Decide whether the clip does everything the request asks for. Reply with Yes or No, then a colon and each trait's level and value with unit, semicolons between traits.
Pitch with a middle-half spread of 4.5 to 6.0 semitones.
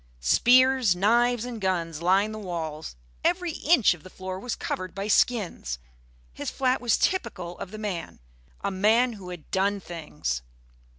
Yes: average, 5.3 semitones